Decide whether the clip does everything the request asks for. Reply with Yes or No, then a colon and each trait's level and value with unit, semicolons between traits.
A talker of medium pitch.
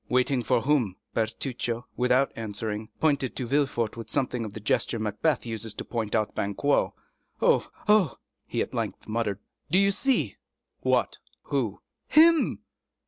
No: low, 120 Hz